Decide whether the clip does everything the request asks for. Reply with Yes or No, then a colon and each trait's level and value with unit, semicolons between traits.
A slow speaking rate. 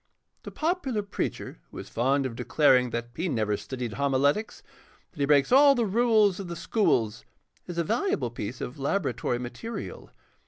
No: average, 170 wpm